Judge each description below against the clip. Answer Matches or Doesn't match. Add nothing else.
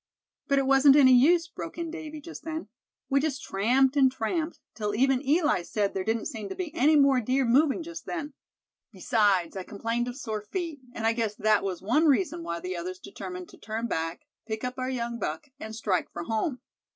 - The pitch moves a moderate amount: Doesn't match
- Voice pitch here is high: Matches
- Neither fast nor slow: Doesn't match